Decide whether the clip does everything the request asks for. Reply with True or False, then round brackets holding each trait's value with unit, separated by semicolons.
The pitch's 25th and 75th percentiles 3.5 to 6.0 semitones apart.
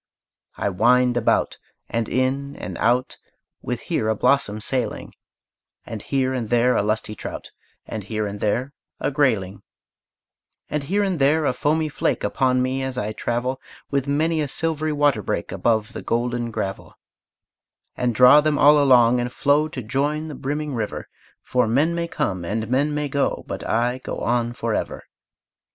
True (3.8 semitones)